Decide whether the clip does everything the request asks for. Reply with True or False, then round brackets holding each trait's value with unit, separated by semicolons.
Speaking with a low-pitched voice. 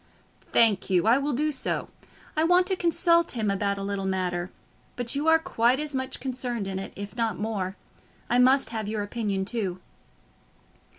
False (230 Hz)